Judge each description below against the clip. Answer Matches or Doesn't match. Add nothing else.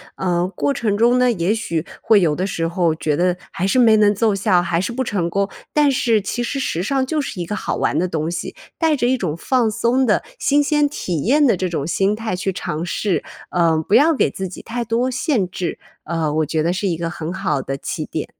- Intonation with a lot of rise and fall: Matches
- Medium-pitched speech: Doesn't match